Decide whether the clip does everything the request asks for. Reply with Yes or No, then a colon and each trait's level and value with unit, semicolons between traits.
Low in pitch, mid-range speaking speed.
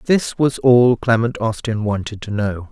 Yes: low, 115 Hz; average, 175 wpm